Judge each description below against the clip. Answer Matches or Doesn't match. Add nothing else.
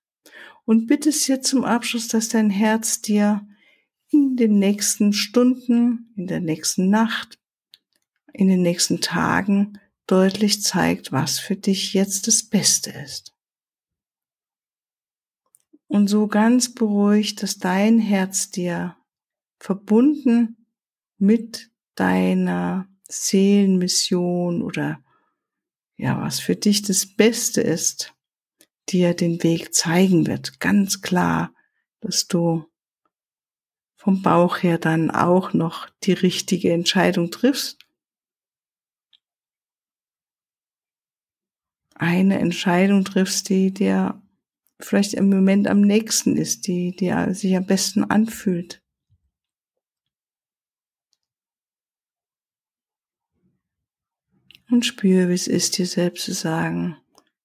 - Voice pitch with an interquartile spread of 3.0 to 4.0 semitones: Matches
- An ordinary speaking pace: Doesn't match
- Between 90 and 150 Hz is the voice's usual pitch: Doesn't match